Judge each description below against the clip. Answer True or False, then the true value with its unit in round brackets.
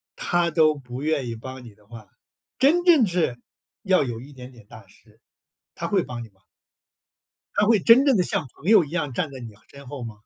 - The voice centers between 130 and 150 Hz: True (140 Hz)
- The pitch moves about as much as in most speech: False (7.0 semitones)